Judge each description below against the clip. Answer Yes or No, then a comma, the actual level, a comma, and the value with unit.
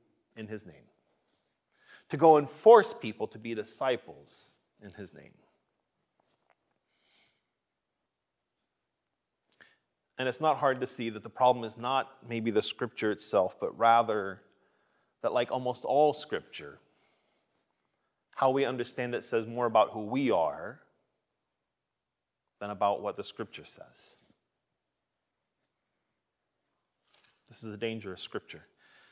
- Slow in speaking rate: Yes, slow, 115 wpm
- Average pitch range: Yes, average, 3.6 semitones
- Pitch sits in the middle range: No, low, 115 Hz